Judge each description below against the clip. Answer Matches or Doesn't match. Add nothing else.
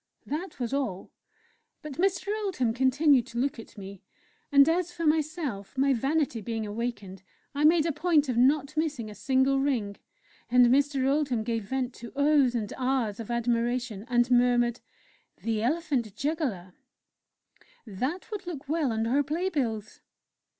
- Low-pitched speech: Doesn't match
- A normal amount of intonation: Matches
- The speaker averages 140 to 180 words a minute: Matches